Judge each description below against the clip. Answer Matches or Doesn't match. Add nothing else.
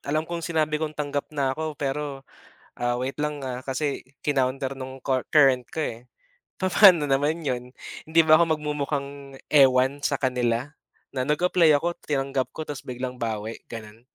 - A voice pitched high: Doesn't match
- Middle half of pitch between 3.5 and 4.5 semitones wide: Doesn't match